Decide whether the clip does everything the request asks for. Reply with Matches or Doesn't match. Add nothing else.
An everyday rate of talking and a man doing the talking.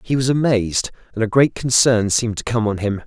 Doesn't match